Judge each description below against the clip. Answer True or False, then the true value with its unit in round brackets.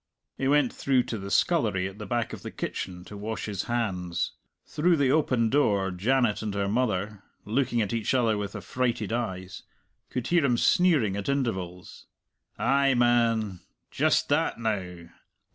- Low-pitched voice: True (110 Hz)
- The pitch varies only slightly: False (4.5 semitones)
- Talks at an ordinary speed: True (160 wpm)